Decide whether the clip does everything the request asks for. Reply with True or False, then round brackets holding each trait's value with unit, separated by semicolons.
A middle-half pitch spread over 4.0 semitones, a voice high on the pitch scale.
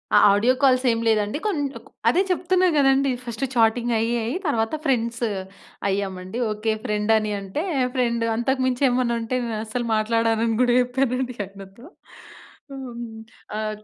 False (2.9 semitones; 235 Hz)